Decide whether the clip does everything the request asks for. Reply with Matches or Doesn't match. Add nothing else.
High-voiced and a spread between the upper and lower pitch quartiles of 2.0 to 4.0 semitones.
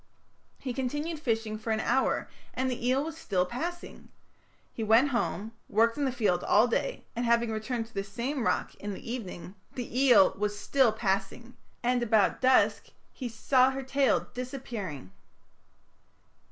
Matches